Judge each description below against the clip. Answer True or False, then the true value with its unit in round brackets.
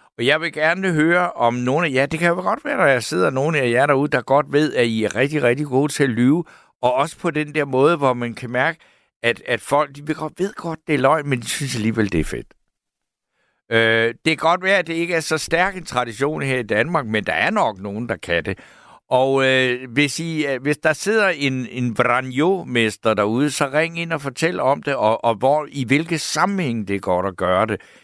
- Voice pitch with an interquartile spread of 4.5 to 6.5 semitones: True (5.2 semitones)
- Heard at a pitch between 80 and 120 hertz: False (140 Hz)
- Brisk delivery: True (250 wpm)